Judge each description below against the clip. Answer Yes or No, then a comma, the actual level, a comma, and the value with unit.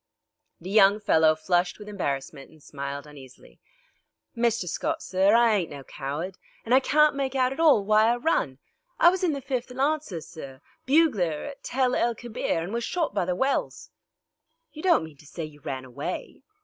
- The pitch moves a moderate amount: No, wide, 9.0 semitones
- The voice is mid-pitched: No, high, 210 Hz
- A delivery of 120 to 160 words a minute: No, average, 190 wpm